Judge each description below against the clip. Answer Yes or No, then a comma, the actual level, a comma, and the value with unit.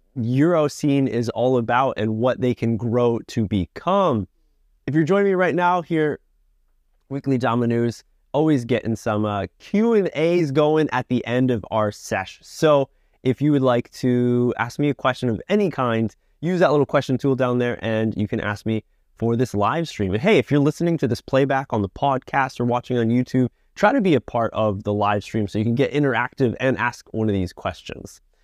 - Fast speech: Yes, fast, 210 wpm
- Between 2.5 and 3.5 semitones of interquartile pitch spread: No, average, 4.2 semitones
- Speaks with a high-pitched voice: No, low, 125 Hz